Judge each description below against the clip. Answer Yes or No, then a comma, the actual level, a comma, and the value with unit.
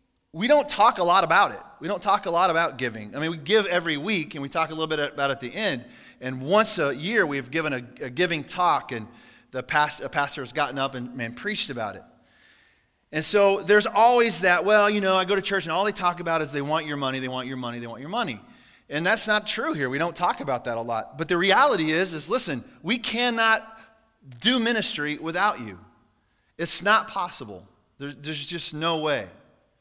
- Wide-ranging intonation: Yes, wide, 7.2 semitones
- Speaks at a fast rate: Yes, fast, 235 wpm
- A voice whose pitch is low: No, medium, 160 Hz